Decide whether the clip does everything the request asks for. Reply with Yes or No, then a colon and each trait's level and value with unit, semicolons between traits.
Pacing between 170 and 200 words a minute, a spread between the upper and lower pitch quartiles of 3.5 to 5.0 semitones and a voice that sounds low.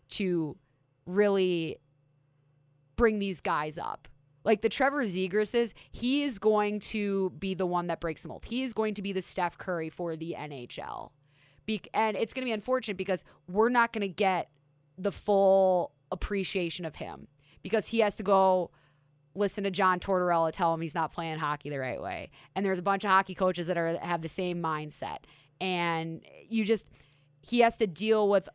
No: average, 185 wpm; average, 4.5 semitones; medium, 185 Hz